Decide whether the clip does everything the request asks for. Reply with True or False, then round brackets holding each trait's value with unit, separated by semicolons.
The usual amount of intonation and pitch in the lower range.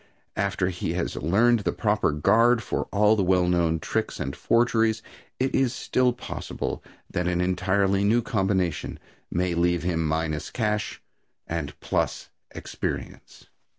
True (4.2 semitones; 95 Hz)